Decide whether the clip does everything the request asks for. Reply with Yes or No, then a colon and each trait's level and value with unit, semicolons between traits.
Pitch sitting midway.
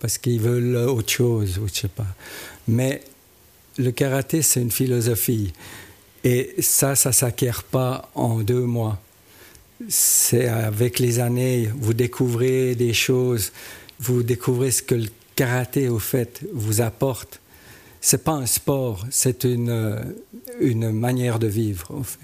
No: low, 120 Hz